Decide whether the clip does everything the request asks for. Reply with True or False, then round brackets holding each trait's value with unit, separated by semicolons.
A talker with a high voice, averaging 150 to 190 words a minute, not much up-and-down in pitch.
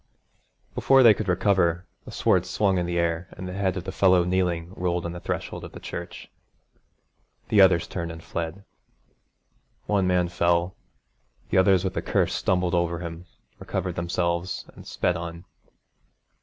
False (90 Hz; 160 wpm; 1.6 semitones)